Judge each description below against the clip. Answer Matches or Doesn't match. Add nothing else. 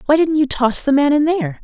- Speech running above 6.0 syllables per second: Matches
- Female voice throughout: Matches